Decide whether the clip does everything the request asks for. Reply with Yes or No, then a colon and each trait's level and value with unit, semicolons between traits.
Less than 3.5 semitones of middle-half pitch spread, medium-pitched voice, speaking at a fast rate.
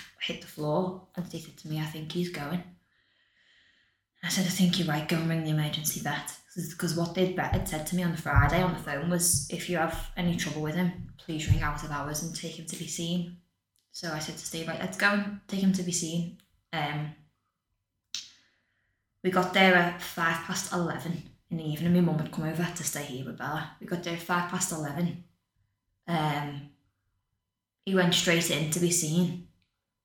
Yes: average, 2.9 semitones; medium, 165 Hz; fast, 210 wpm